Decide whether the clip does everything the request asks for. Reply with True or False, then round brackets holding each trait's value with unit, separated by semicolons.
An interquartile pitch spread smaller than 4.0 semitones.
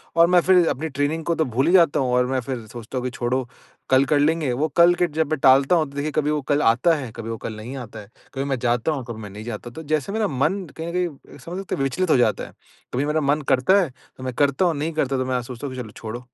False (4.3 semitones)